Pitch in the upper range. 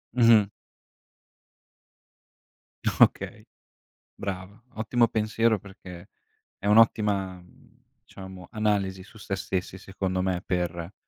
No: low, 100 Hz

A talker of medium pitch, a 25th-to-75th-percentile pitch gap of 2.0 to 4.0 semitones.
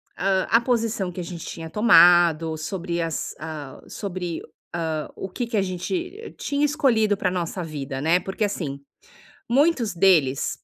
No: medium, 180 Hz; average, 5.2 semitones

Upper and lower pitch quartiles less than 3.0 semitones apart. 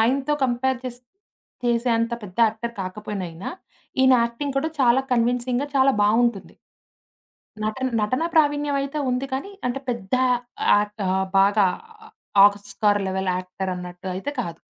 No: average, 4.5 semitones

